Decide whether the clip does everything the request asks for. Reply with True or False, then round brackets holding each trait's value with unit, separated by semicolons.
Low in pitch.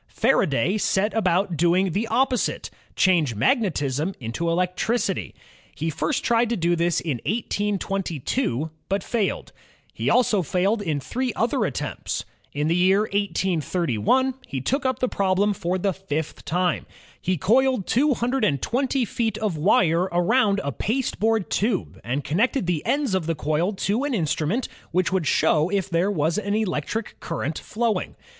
False (190 Hz)